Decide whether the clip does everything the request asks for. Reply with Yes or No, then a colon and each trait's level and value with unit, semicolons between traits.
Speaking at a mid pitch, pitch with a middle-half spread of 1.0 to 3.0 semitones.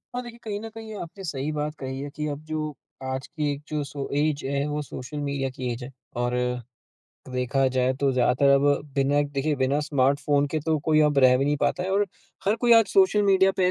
Yes: medium, 145 Hz; average, 2.7 semitones